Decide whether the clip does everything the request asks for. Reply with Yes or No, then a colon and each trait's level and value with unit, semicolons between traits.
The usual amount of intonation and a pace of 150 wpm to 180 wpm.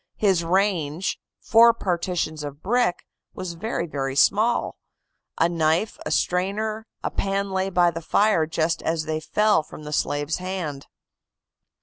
No: average, 4.0 semitones; slow, 135 wpm